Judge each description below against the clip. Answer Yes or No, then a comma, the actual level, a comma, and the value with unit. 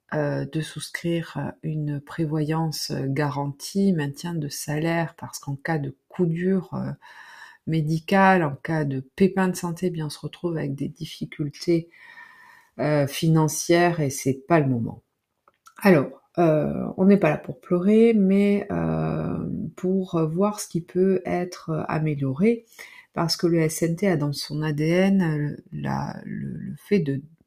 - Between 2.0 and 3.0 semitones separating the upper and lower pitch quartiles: No, average, 4.1 semitones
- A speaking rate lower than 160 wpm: Yes, average, 150 wpm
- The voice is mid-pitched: Yes, medium, 160 Hz